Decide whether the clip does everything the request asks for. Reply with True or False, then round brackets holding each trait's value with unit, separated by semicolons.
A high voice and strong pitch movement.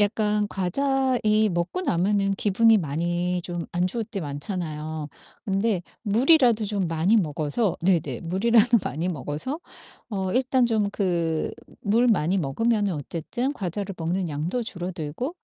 False (195 Hz; 4.8 semitones)